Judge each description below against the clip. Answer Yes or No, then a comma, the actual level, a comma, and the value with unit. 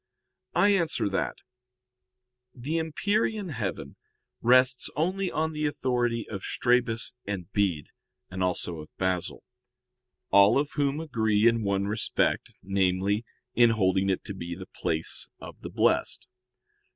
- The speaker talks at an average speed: No, slow, 130 wpm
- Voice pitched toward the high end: No, low, 110 Hz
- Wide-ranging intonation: Yes, wide, 6.9 semitones